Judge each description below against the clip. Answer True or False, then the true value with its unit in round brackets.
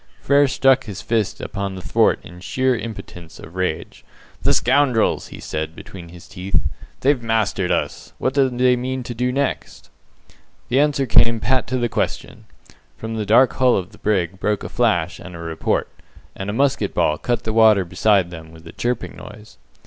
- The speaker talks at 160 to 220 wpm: True (185 wpm)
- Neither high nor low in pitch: False (110 Hz)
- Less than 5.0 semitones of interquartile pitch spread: False (5.4 semitones)